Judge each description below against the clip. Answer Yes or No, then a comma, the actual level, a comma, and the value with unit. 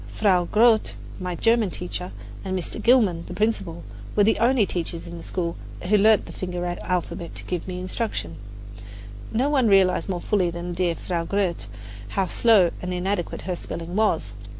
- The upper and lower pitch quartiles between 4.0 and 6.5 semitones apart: No, average, 3.4 semitones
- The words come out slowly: No, average, 175 wpm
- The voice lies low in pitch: No, medium, 185 Hz